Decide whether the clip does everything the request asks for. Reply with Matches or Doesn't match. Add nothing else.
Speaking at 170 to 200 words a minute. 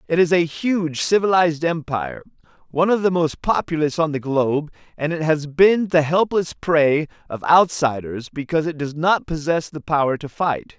Matches